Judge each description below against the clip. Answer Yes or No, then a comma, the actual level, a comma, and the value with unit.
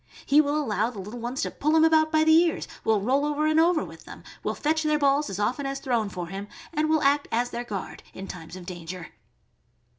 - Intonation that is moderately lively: No, wide, 6.9 semitones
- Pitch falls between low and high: No, very high, 275 Hz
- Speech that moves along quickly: Yes, fast, 240 wpm